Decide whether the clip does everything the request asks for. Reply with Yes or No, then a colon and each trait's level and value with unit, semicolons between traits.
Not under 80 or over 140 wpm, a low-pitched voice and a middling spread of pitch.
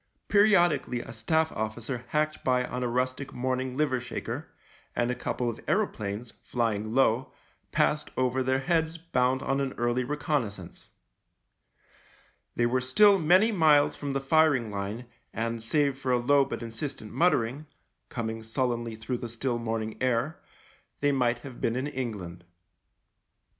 No: average, 155 wpm; low, 125 Hz; average, 3.7 semitones